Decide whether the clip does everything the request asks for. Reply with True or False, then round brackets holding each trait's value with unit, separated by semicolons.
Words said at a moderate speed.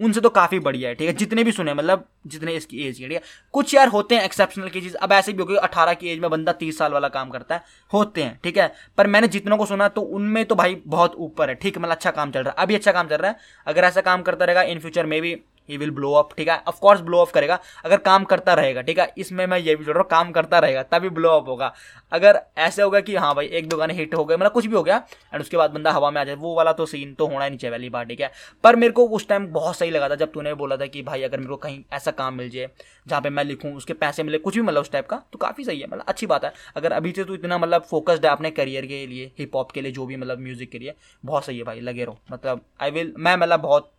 False (310 wpm)